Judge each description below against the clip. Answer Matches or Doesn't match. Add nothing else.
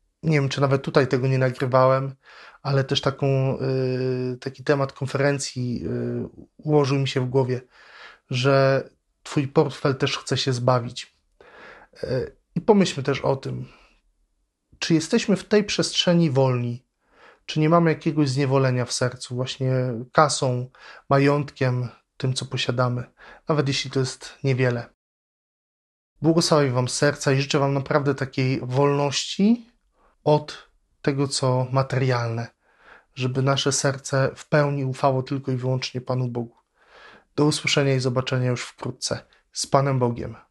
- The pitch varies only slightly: Matches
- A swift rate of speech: Doesn't match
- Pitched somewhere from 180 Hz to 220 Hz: Doesn't match